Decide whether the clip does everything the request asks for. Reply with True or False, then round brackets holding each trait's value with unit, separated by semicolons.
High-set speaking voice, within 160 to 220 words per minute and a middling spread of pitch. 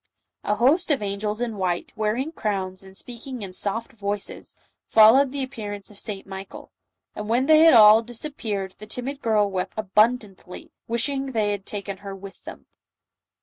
True (215 Hz; 175 wpm; 3.7 semitones)